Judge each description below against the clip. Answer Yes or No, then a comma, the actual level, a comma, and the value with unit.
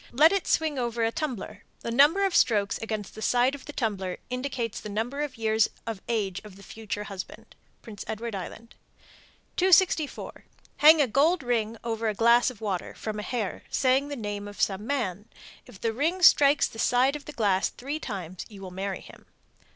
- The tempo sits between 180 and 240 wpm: Yes, average, 195 wpm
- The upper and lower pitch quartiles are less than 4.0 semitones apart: No, average, 5.2 semitones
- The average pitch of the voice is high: Yes, high, 230 Hz